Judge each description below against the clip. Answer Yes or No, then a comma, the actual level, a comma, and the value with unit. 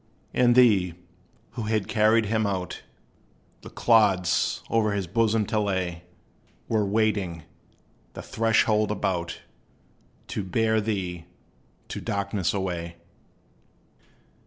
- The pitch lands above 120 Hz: No, low, 105 Hz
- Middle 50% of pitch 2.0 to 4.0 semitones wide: Yes, average, 3.2 semitones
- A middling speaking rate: No, slow, 105 wpm